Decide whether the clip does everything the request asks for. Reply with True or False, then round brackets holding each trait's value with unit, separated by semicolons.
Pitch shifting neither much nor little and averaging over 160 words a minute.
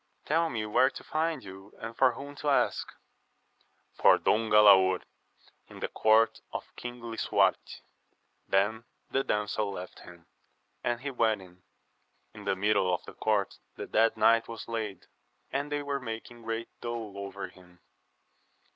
False (3.4 semitones; 155 wpm)